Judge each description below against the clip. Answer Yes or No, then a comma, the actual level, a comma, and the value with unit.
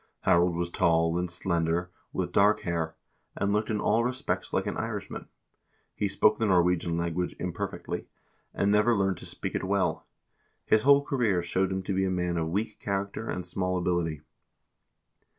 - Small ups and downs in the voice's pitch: No, average, 3.1 semitones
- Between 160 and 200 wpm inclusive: Yes, average, 175 wpm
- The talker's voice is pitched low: Yes, very low, 90 Hz